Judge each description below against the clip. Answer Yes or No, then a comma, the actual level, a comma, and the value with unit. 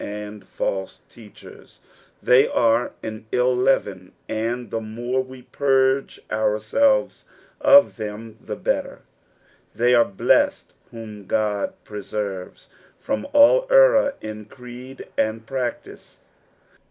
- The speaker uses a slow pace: Yes, slow, 110 wpm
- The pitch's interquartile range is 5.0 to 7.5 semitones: No, average, 3.6 semitones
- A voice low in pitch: Yes, low, 115 Hz